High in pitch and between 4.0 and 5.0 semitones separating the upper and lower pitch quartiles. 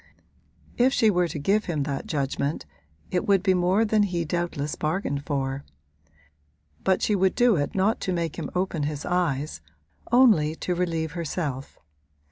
No: medium, 175 Hz; average, 4.5 semitones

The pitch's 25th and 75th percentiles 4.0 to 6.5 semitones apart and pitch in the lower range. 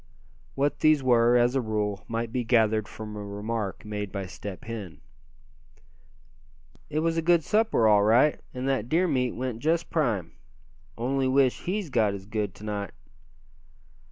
Yes: average, 4.6 semitones; low, 115 Hz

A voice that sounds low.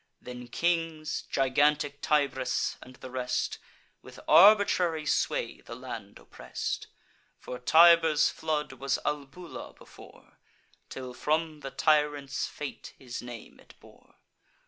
No: medium, 145 Hz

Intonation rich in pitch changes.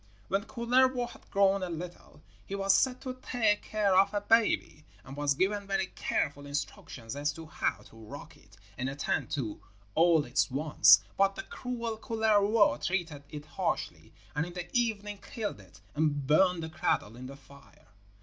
Yes: wide, 6.4 semitones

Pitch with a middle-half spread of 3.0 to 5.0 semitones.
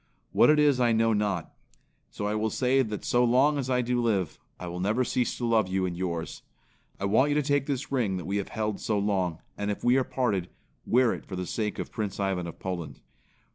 Yes: average, 4.7 semitones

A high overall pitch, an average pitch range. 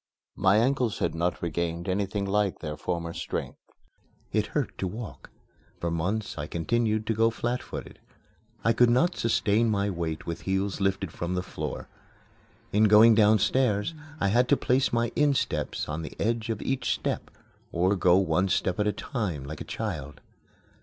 No: low, 100 Hz; average, 4.7 semitones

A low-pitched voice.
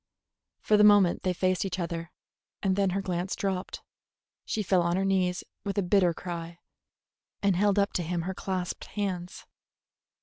No: medium, 185 Hz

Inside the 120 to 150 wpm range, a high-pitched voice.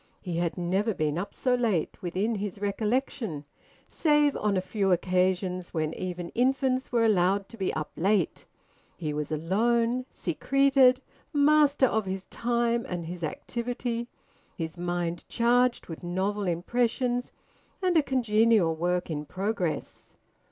Yes: slow, 135 wpm; high, 205 Hz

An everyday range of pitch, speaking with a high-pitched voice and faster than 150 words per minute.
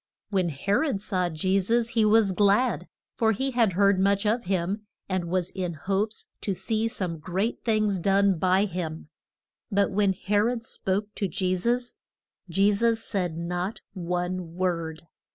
Yes: average, 3.0 semitones; high, 195 Hz; average, 165 wpm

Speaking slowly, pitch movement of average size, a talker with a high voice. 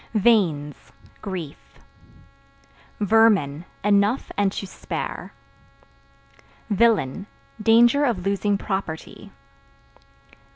Yes: slow, 70 wpm; average, 3.7 semitones; high, 200 Hz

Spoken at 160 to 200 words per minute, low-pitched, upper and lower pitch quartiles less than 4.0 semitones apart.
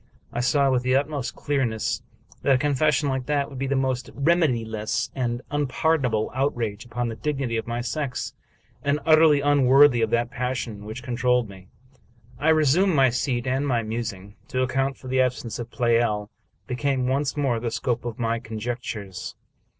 Yes: average, 175 wpm; low, 125 Hz; average, 3.0 semitones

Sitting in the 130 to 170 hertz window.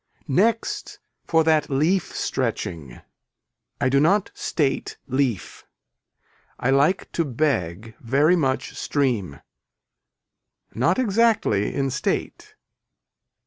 Yes: medium, 140 Hz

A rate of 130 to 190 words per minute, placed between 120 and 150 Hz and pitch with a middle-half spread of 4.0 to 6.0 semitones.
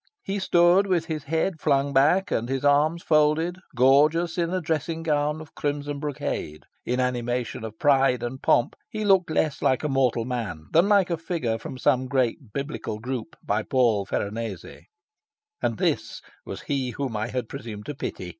Yes: average, 175 wpm; medium, 140 Hz; average, 4.9 semitones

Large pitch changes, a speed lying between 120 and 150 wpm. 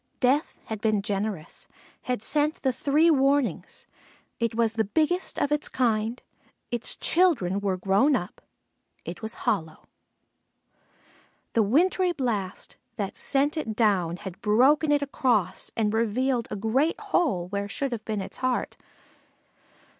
Yes: wide, 5.7 semitones; average, 140 wpm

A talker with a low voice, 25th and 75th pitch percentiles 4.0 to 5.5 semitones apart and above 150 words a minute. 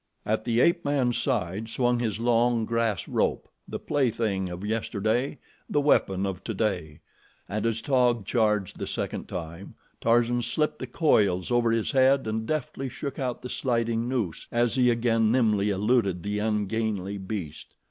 No: low, 115 Hz; average, 3.1 semitones; average, 160 wpm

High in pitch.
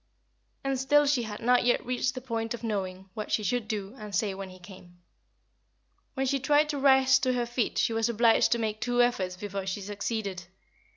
Yes: high, 225 Hz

